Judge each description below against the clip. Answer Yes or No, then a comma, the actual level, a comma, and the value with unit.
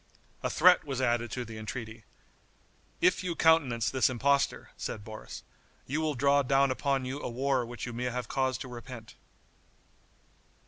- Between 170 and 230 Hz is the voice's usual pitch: No, low, 130 Hz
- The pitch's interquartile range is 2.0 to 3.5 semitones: Yes, average, 2.8 semitones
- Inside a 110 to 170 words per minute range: Yes, average, 165 wpm